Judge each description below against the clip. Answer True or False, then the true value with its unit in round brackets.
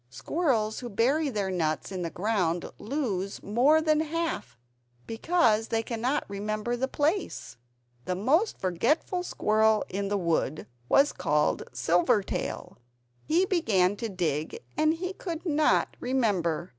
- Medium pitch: False (220 Hz)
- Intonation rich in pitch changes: True (8.4 semitones)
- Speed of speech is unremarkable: False (130 wpm)